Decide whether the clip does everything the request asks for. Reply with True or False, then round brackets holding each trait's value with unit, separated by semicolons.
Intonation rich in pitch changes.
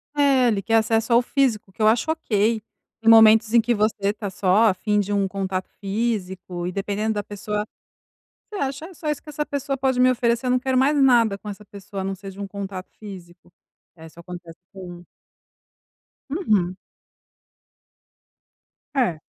False (4.2 semitones)